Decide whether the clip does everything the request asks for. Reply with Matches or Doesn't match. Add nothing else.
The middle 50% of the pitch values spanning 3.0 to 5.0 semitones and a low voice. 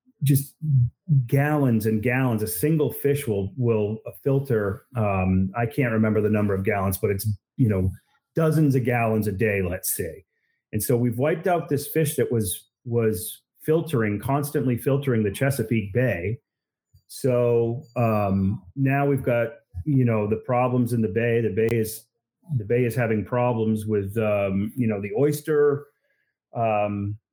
Matches